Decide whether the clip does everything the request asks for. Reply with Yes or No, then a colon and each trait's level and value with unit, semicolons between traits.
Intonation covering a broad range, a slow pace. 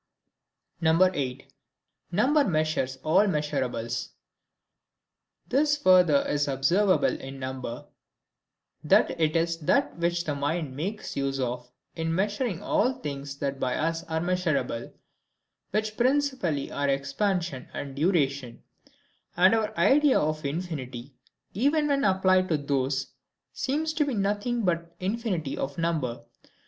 Yes: wide, 6.5 semitones; slow, 125 wpm